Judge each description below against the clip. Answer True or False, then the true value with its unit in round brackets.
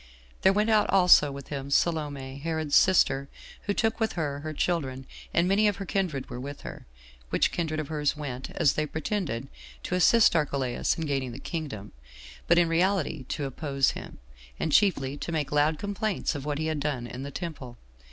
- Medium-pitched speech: True (150 Hz)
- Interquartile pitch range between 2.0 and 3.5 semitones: False (4.1 semitones)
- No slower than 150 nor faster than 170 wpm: False (190 wpm)